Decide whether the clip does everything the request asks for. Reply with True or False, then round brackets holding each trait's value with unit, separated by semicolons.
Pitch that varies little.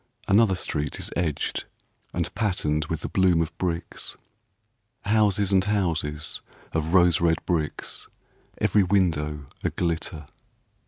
False (3.6 semitones)